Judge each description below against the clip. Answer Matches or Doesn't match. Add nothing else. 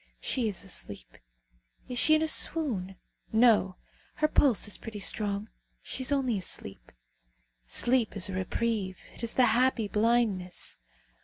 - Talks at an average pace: Matches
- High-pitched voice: Matches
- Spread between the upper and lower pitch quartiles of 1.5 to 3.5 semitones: Doesn't match